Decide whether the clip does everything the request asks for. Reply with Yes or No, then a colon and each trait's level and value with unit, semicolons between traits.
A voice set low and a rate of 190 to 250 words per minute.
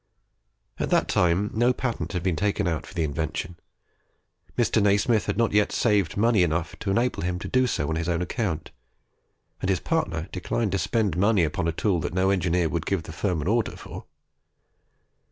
Yes: very low, 95 Hz; average, 195 wpm